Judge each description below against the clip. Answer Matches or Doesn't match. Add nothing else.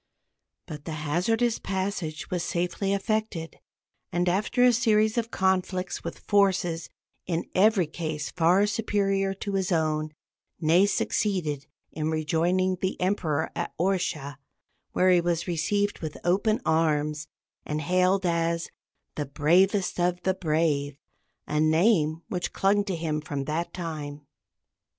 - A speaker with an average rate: Doesn't match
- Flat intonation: Doesn't match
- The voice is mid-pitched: Matches